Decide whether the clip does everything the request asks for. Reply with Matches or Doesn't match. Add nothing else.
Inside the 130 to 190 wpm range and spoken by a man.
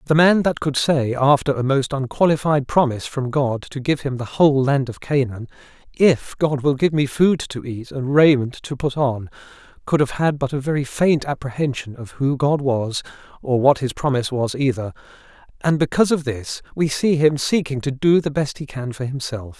Doesn't match